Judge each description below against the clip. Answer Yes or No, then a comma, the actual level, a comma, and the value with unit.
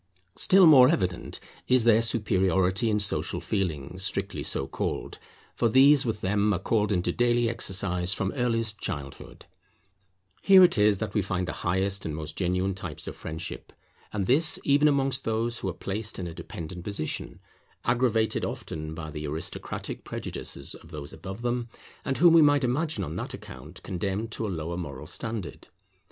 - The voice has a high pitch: No, low, 100 Hz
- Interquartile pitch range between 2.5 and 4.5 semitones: No, average, 5.0 semitones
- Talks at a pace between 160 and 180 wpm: Yes, average, 170 wpm